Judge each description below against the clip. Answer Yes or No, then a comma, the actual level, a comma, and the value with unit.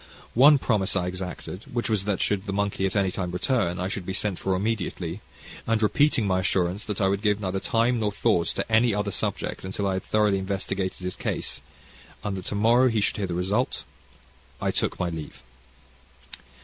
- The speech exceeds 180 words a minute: Yes, average, 200 wpm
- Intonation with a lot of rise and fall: No, narrow, 2.5 semitones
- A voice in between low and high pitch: No, low, 100 Hz